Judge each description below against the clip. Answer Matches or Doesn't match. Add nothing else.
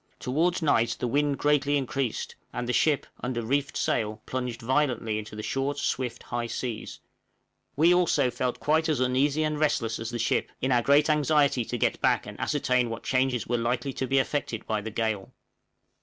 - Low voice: Matches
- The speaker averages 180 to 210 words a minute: Matches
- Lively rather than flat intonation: Doesn't match